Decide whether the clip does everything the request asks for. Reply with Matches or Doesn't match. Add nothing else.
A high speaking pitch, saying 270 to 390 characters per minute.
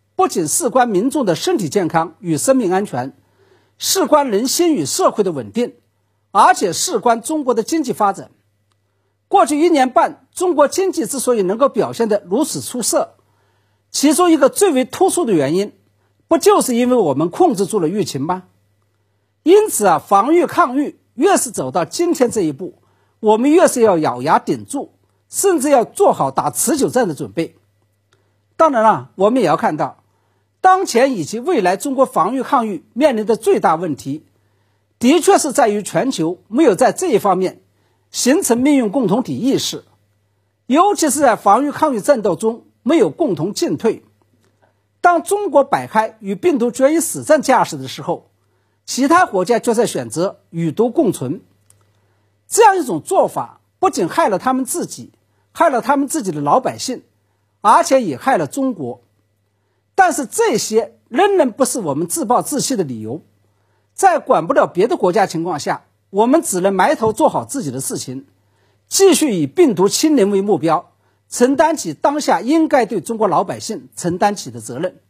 Doesn't match